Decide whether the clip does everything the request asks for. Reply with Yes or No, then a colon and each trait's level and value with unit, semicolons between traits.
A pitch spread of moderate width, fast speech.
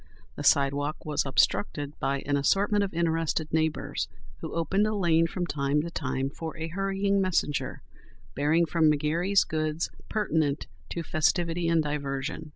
No: average, 3.0 semitones; average, 150 wpm